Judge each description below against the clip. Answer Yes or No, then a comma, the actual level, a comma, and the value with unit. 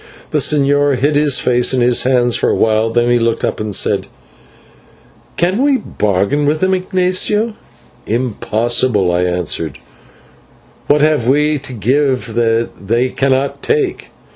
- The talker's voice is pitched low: Yes, low, 130 Hz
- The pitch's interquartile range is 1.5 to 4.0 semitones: No, average, 4.6 semitones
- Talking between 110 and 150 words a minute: Yes, average, 140 wpm